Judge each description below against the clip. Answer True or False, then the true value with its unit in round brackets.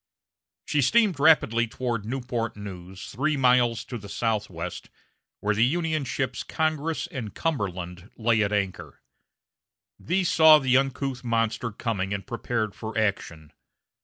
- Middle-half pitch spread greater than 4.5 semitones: True (5.0 semitones)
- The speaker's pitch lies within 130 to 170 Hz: False (115 Hz)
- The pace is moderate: False (130 wpm)